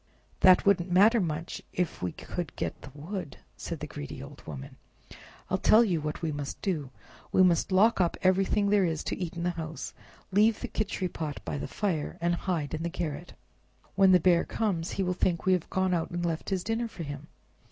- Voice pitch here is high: No, medium, 175 Hz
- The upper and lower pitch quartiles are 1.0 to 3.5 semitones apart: Yes, average, 3.2 semitones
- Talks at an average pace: No, fast, 210 wpm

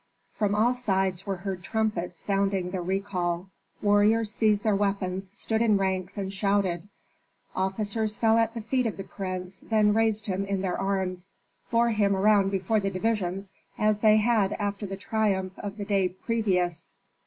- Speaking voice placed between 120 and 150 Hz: No, high, 200 Hz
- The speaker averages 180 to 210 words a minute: No, average, 165 wpm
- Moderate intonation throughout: No, narrow, 2.1 semitones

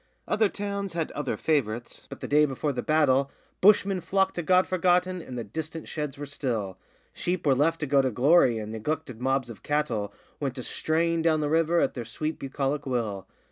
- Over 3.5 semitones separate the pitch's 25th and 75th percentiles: Yes, average, 4.7 semitones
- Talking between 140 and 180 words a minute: No, average, 200 wpm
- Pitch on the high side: No, medium, 150 Hz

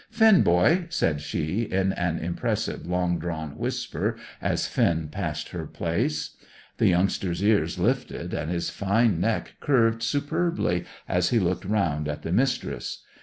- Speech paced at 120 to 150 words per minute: Yes, average, 145 wpm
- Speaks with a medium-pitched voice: No, very low, 90 Hz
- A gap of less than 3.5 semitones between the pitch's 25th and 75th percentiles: No, average, 5.2 semitones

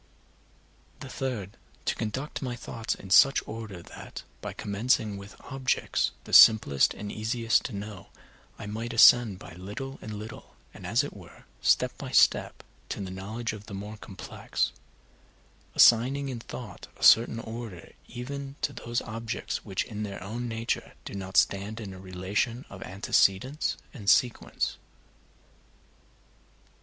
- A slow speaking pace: No, average, 150 wpm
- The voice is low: Yes, low, 110 Hz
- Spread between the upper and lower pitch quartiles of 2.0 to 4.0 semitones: Yes, average, 3.4 semitones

